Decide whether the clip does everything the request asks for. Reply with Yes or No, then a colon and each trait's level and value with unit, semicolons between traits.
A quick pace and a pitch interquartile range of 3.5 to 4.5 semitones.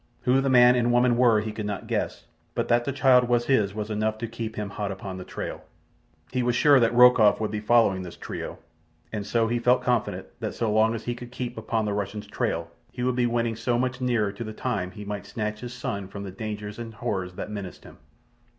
No: fast, 240 wpm; average, 2.8 semitones